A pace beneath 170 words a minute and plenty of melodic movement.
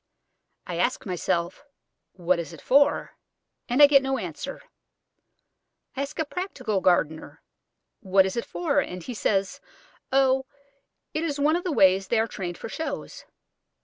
Yes: average, 155 wpm; wide, 7.3 semitones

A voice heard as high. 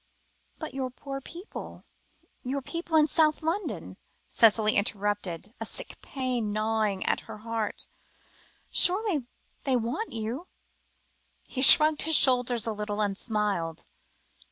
Yes: high, 240 Hz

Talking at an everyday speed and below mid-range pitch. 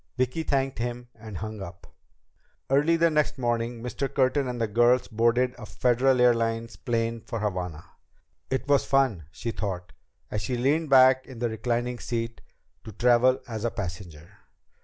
Yes: average, 160 wpm; low, 120 Hz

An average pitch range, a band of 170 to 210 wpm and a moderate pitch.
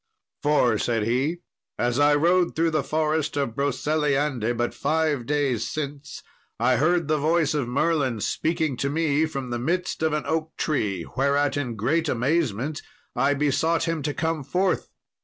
No: average, 3.7 semitones; average, 160 wpm; medium, 145 Hz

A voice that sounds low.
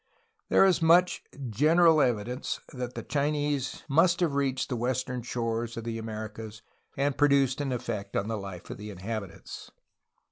Yes: low, 125 Hz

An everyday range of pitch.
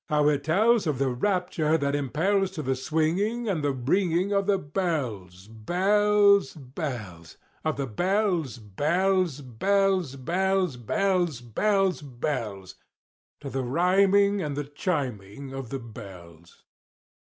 No: wide, 7.1 semitones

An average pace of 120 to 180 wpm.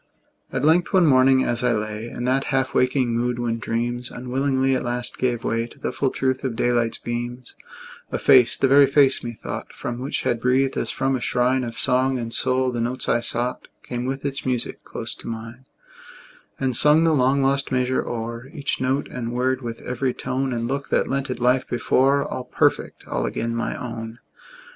No: average, 200 wpm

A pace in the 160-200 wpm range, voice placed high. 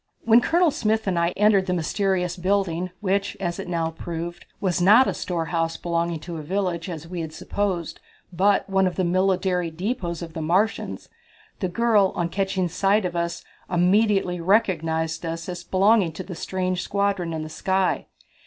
No: average, 175 wpm; medium, 180 Hz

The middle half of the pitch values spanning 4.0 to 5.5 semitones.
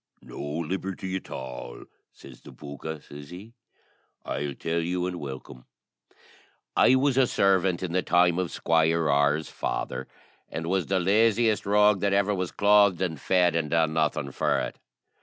Yes: average, 4.4 semitones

